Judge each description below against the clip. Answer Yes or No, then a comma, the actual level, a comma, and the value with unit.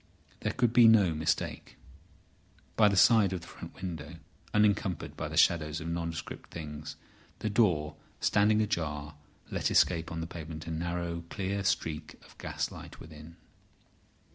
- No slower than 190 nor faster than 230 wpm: No, average, 150 wpm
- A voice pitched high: No, very low, 85 Hz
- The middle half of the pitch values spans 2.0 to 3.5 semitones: No, average, 4.1 semitones